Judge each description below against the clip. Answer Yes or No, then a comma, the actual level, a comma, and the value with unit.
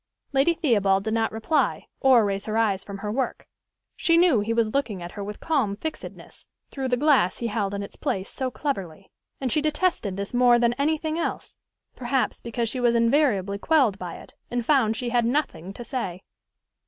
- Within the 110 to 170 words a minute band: No, average, 200 wpm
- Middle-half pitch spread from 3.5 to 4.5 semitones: No, average, 5.2 semitones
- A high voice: Yes, high, 235 Hz